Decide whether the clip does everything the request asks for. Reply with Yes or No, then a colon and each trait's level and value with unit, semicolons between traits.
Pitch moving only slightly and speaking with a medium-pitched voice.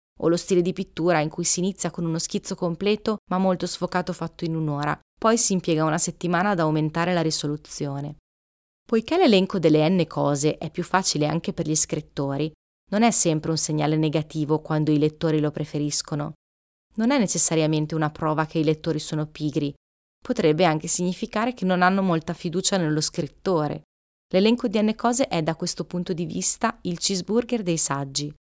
No: average, 3.3 semitones; medium, 165 Hz